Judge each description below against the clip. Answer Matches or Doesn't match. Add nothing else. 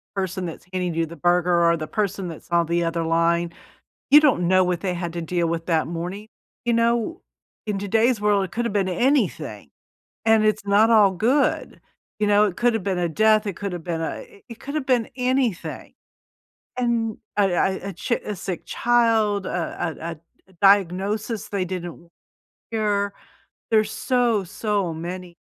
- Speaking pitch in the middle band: Doesn't match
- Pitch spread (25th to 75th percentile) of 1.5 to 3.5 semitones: Doesn't match